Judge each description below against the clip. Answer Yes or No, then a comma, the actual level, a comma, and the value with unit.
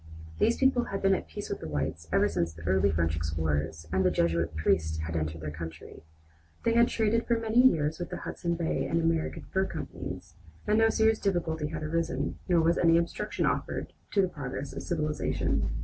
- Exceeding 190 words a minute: Yes, average, 200 wpm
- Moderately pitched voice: Yes, medium, 155 Hz